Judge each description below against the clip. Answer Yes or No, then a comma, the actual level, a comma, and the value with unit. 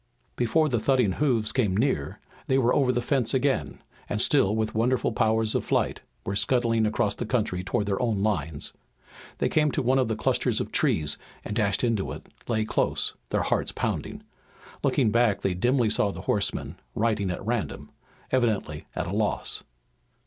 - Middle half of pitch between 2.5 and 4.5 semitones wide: Yes, average, 3.7 semitones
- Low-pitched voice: Yes, low, 110 Hz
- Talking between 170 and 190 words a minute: Yes, average, 180 wpm